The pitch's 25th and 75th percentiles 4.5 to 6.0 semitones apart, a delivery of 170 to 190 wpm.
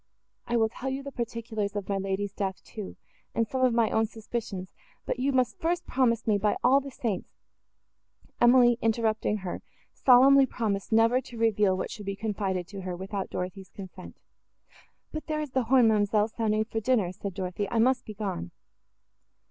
No: average, 3.6 semitones; average, 180 wpm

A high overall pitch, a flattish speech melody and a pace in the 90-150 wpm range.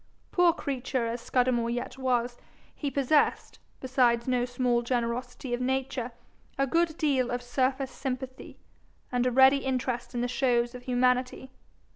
Yes: very high, 255 Hz; narrow, 1.4 semitones; average, 145 wpm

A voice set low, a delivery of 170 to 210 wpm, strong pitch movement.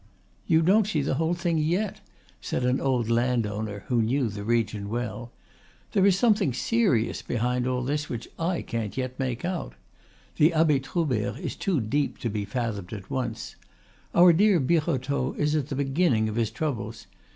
Yes: low, 130 Hz; average, 175 wpm; wide, 5.8 semitones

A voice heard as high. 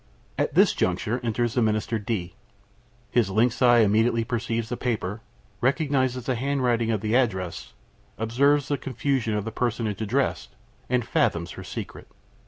No: low, 115 Hz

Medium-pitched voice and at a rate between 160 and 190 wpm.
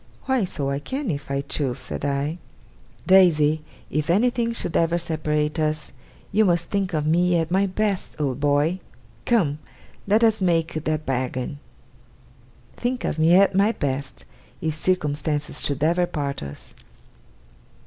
No: medium, 160 Hz; average, 150 wpm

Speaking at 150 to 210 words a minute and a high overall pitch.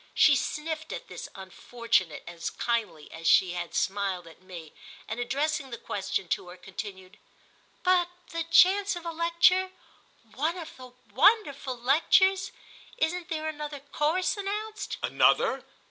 No: slow, 135 wpm; very high, 290 Hz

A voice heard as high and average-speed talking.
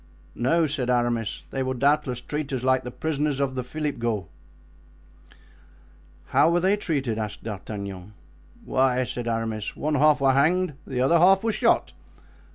No: low, 130 Hz; average, 165 wpm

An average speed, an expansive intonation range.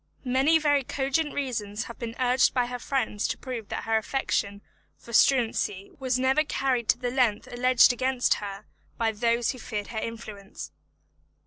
No: average, 165 wpm; average, 3.0 semitones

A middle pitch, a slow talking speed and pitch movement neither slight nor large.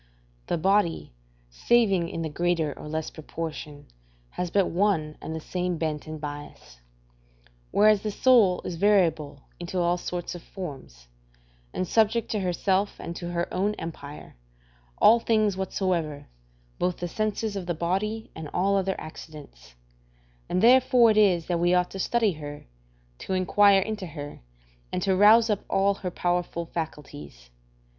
No: medium, 180 Hz; average, 155 wpm; average, 4.1 semitones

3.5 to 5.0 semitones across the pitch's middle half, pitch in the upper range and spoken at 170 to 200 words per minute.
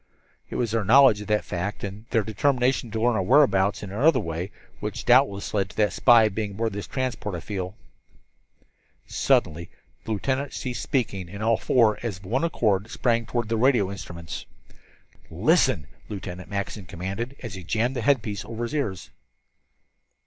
No: average, 3.8 semitones; low, 110 Hz; average, 175 wpm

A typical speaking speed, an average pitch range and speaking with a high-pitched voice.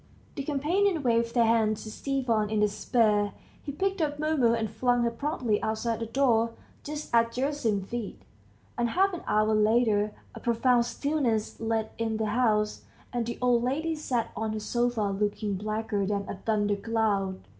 Yes: average, 165 wpm; average, 3.1 semitones; high, 230 Hz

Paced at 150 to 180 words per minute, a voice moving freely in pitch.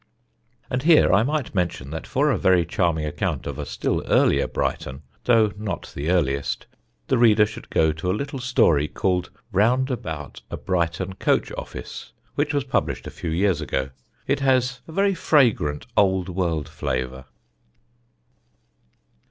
Yes: average, 155 wpm; wide, 7.9 semitones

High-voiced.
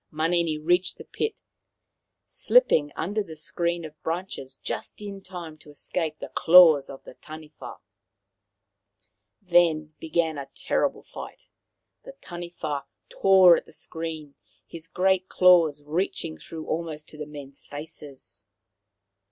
No: medium, 160 Hz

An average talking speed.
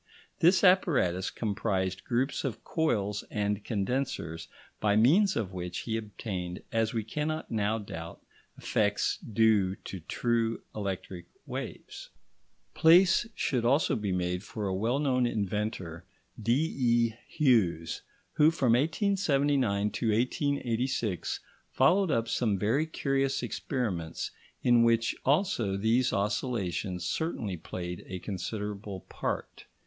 No: slow, 115 wpm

